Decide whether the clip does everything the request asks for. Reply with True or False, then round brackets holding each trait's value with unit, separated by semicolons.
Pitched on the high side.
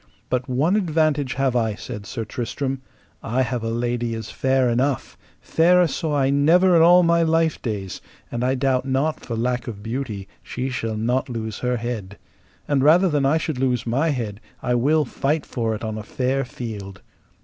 False (130 Hz)